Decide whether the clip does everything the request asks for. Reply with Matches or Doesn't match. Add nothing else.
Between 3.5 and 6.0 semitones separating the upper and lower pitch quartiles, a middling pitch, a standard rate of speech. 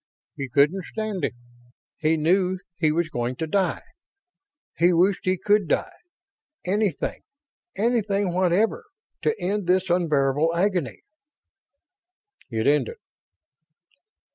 Doesn't match